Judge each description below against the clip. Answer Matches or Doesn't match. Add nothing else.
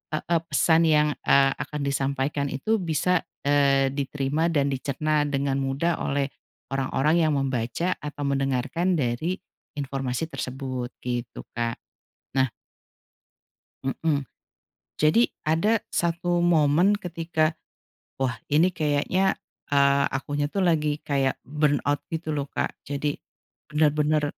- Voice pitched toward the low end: Doesn't match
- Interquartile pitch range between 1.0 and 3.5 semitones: Matches